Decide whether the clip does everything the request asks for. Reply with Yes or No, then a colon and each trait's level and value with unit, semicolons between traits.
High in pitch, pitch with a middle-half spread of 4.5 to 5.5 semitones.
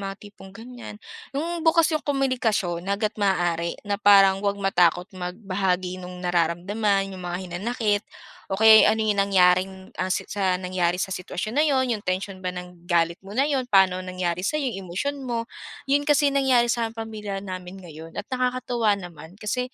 No: high, 195 Hz; average, 4.1 semitones